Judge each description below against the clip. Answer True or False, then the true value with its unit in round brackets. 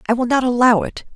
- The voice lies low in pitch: False (240 Hz)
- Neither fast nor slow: False (260 wpm)